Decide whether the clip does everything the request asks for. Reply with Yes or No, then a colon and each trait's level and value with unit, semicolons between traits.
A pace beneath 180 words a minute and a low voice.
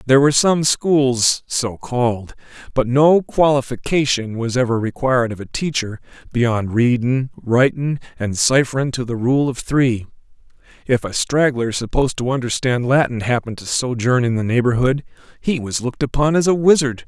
Yes: average, 155 wpm; low, 125 Hz